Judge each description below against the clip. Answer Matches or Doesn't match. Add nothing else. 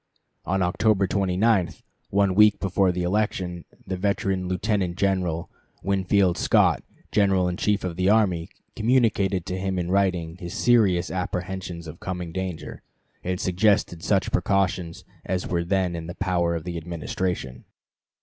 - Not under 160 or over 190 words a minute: Doesn't match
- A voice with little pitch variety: Matches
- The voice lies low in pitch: Matches